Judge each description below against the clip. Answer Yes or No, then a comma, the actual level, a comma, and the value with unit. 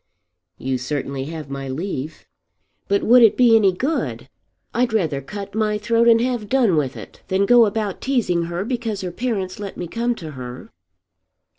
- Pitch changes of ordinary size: No, wide, 6.5 semitones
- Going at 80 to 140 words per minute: No, average, 175 wpm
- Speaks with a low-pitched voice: No, high, 200 Hz